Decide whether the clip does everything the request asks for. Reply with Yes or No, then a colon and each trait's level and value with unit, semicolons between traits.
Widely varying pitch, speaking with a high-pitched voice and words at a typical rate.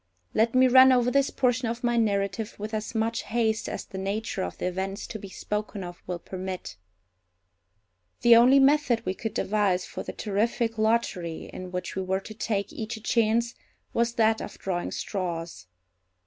No: average, 3.5 semitones; high, 220 Hz; average, 180 wpm